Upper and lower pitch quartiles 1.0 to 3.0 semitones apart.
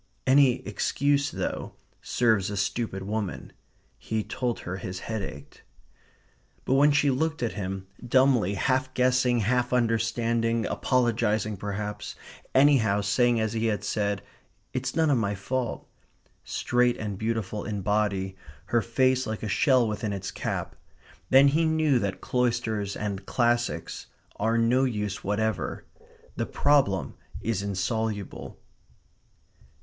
No: average, 3.7 semitones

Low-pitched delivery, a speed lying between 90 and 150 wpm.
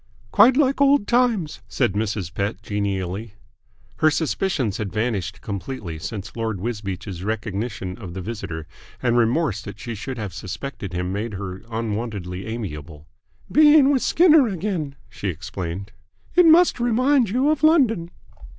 Yes: low, 110 Hz; average, 140 wpm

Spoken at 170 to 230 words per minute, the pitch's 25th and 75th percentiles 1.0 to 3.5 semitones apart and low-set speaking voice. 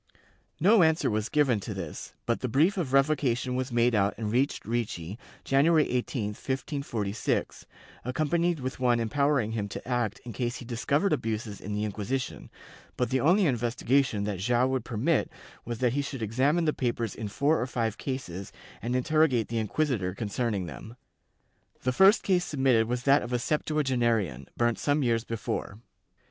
No: average, 175 wpm; average, 4.1 semitones; low, 125 Hz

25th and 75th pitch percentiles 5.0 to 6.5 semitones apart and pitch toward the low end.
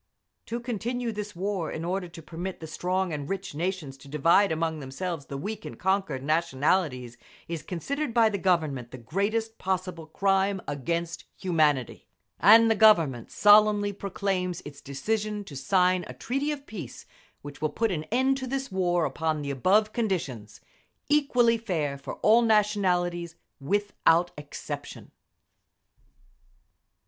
No: average, 5.3 semitones; medium, 185 Hz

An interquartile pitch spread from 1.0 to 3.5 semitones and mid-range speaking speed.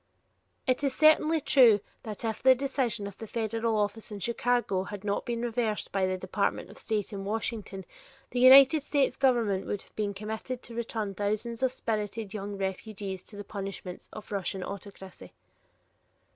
Yes: average, 3.2 semitones; average, 170 wpm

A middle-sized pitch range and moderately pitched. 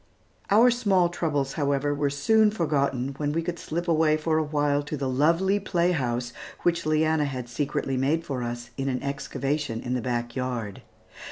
Yes: average, 4.0 semitones; medium, 145 Hz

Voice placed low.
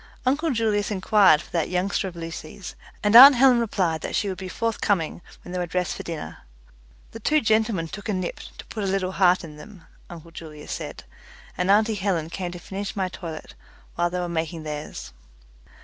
No: medium, 185 Hz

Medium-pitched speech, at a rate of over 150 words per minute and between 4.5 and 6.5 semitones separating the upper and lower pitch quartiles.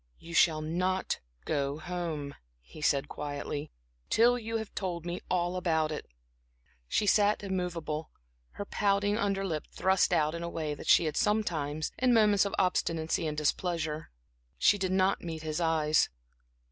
No: medium, 170 Hz; average, 160 wpm; average, 3.9 semitones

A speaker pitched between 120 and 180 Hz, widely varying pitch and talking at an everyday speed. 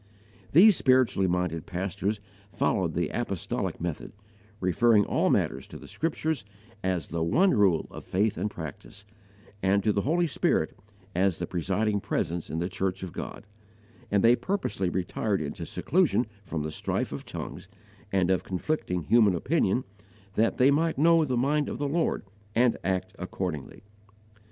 No: low, 100 Hz; wide, 6.3 semitones; average, 155 wpm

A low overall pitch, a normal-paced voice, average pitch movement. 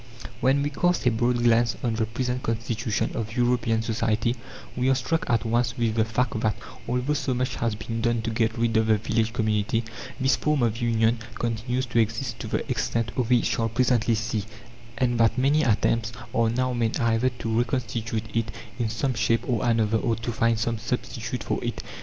No: low, 115 Hz; average, 195 wpm; narrow, 1.7 semitones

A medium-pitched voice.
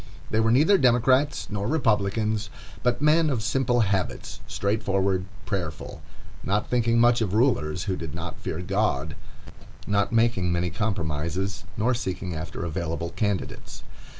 No: low, 105 Hz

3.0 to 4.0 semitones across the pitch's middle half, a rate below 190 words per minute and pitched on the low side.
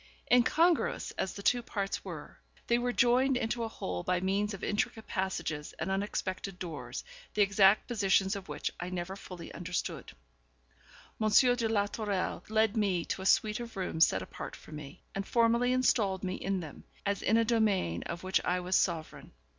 No: average, 3.6 semitones; average, 180 wpm; high, 195 Hz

